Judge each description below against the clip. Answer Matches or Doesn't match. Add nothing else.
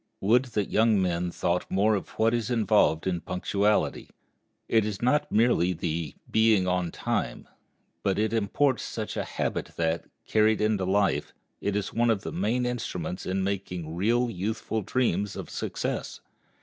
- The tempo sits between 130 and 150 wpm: Doesn't match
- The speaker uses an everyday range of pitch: Matches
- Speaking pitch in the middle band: Doesn't match